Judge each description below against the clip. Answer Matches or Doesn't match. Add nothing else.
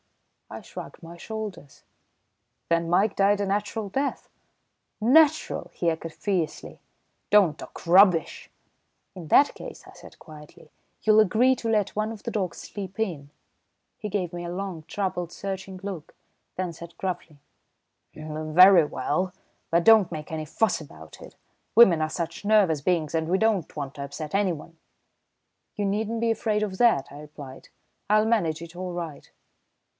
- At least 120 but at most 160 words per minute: Matches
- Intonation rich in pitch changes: Doesn't match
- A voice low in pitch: Doesn't match